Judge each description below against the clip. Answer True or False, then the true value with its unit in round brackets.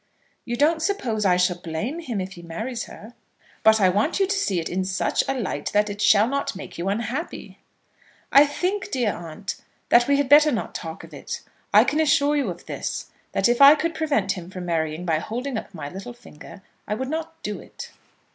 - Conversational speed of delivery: False (215 wpm)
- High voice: True (220 Hz)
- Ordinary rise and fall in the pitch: False (7.4 semitones)